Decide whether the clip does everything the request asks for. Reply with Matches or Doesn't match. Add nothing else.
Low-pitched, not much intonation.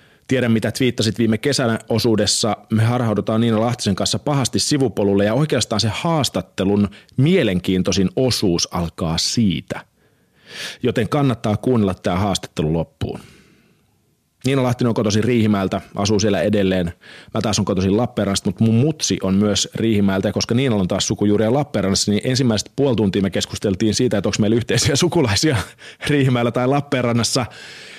Doesn't match